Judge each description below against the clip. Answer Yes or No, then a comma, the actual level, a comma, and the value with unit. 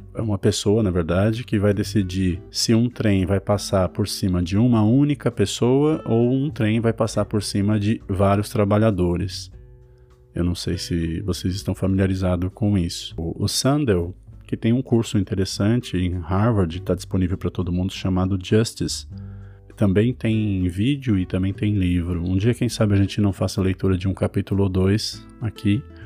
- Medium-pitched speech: No, low, 100 Hz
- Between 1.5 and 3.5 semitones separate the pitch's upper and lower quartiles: Yes, average, 2.9 semitones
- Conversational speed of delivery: Yes, average, 175 wpm